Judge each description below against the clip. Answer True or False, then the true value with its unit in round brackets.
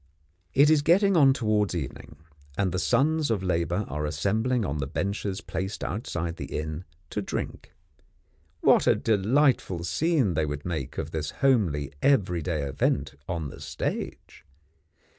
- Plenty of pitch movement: True (8.2 semitones)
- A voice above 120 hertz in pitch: False (95 Hz)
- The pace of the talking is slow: False (145 wpm)